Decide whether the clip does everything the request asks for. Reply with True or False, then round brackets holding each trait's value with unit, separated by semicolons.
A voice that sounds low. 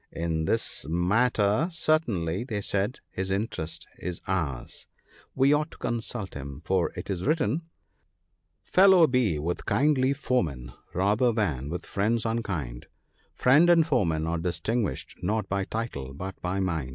True (100 Hz)